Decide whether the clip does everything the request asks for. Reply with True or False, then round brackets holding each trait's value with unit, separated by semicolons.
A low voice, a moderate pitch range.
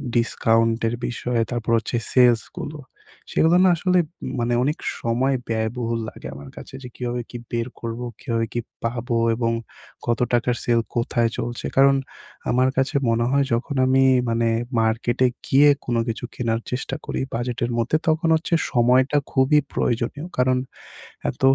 False (120 Hz; 2.2 semitones)